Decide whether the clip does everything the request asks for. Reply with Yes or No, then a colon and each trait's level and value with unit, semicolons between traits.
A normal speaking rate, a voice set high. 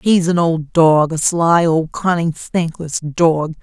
No: average, 165 wpm; medium, 165 Hz